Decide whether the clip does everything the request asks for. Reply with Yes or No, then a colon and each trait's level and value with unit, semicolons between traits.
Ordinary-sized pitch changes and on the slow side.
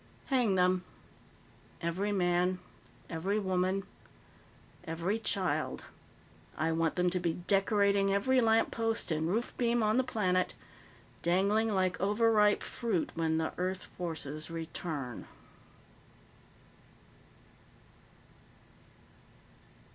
Yes: average, 3.8 semitones; slow, 95 wpm